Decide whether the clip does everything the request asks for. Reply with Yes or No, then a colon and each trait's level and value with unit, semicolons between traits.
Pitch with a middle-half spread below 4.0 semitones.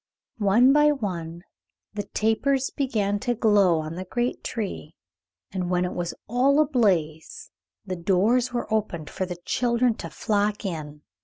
No: wide, 5.4 semitones